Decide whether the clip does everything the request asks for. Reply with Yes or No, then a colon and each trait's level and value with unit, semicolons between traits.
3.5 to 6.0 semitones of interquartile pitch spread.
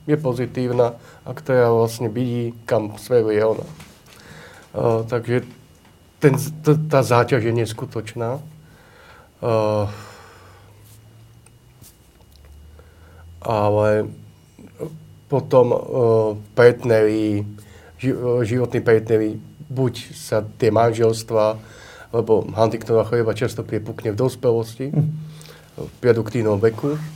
No: average, 2.8 semitones